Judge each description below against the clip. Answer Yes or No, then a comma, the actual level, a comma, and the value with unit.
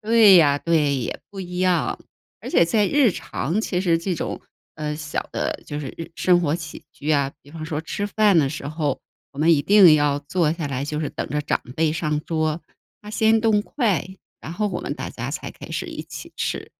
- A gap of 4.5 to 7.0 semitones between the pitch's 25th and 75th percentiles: No, average, 4.1 semitones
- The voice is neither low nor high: Yes, medium, 165 Hz